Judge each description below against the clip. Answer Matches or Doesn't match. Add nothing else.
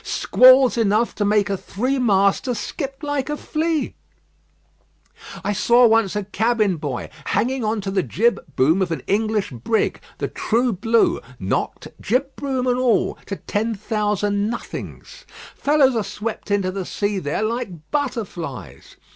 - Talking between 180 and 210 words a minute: Doesn't match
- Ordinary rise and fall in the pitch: Matches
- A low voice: Doesn't match